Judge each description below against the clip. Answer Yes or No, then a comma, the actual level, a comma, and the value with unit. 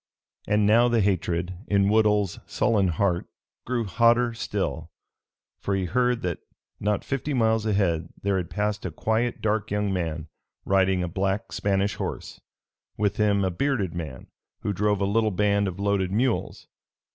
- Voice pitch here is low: Yes, low, 100 Hz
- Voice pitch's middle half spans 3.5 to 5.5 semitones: No, average, 2.7 semitones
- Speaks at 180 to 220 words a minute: No, average, 155 wpm